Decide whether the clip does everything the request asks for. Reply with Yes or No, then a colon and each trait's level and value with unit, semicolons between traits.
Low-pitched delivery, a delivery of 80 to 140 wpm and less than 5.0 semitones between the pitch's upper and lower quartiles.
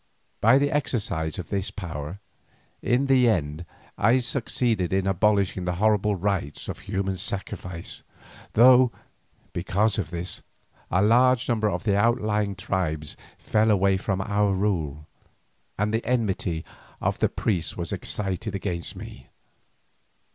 Yes: low, 100 Hz; slow, 135 wpm; average, 3.7 semitones